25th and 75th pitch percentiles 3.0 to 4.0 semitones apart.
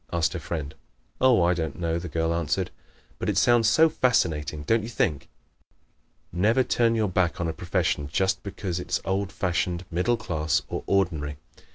No: average, 4.4 semitones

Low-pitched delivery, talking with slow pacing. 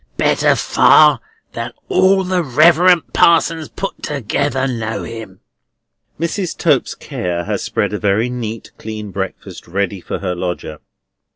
Yes: low, 120 Hz; slow, 130 wpm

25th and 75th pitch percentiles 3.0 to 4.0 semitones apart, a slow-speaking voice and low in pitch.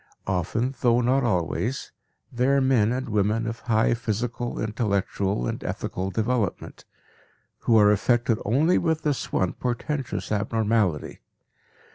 Yes: average, 3.3 semitones; slow, 125 wpm; low, 115 Hz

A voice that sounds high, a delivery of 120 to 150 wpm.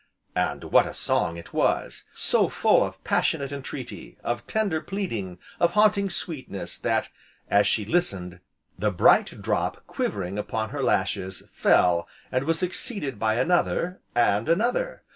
No: low, 125 Hz; average, 145 wpm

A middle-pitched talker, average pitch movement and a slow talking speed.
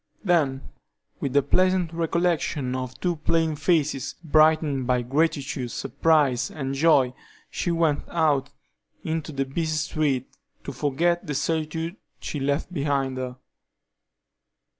Yes: medium, 150 Hz; average, 3.3 semitones; slow, 120 wpm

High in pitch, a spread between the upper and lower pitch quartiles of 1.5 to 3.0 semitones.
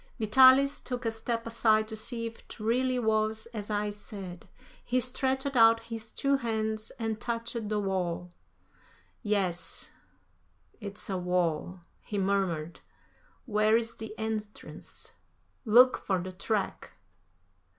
Yes: high, 220 Hz; narrow, 2.5 semitones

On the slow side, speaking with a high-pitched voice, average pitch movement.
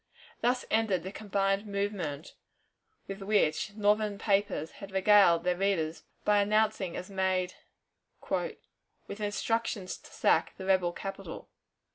No: slow, 120 wpm; high, 195 Hz; narrow, 2.1 semitones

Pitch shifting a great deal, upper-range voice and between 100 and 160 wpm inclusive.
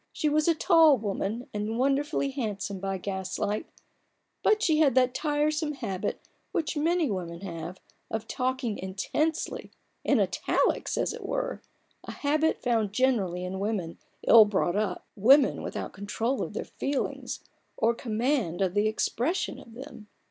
Yes: wide, 6.7 semitones; high, 230 Hz; average, 150 wpm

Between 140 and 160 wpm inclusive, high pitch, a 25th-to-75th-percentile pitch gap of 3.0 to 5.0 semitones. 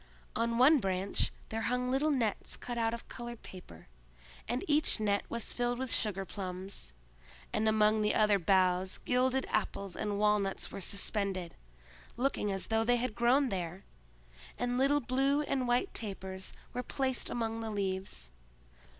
Yes: average, 150 wpm; high, 220 Hz; average, 4.2 semitones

